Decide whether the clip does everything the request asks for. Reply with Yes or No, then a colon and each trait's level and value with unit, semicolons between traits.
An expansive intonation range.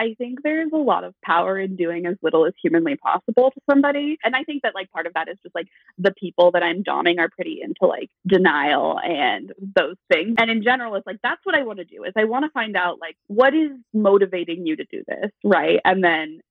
Yes: wide, 7.1 semitones